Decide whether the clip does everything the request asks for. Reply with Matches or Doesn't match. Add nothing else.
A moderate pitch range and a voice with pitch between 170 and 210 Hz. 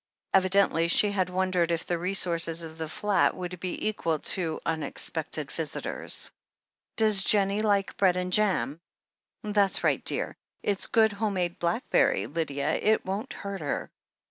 Matches